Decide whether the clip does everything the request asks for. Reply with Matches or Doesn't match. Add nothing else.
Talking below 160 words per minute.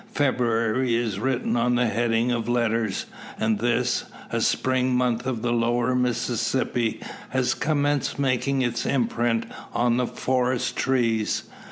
Matches